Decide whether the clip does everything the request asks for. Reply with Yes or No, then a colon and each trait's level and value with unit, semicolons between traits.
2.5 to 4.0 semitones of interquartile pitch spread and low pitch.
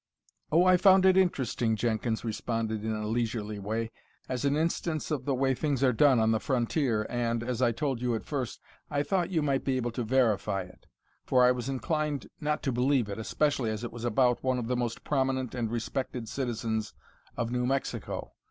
Yes: average, 3.4 semitones; low, 125 Hz